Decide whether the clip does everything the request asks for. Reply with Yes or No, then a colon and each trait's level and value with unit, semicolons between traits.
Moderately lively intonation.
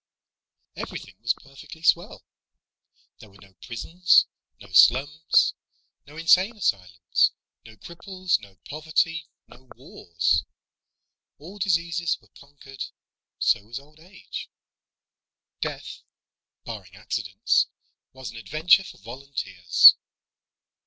No: wide, 7.2 semitones